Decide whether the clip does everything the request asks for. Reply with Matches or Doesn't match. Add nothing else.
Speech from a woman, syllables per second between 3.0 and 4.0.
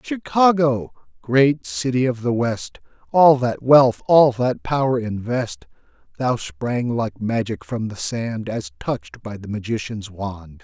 Doesn't match